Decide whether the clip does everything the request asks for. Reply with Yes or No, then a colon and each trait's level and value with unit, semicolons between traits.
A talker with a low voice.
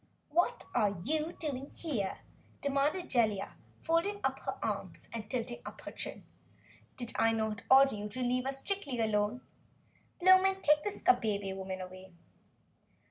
No: very high, 255 Hz